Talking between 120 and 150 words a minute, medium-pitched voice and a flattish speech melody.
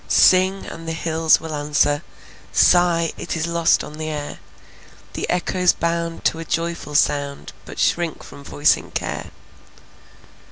Yes: average, 145 wpm; medium, 165 Hz; narrow, 2.1 semitones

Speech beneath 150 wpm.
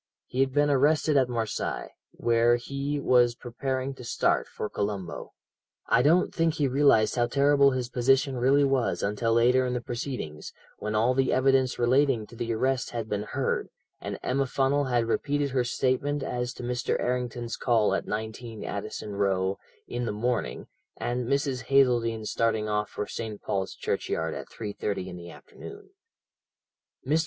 No: average, 165 wpm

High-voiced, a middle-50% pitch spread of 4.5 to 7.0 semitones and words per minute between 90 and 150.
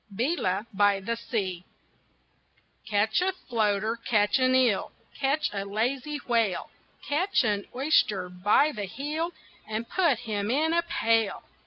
Yes: high, 230 Hz; wide, 5.5 semitones; slow, 135 wpm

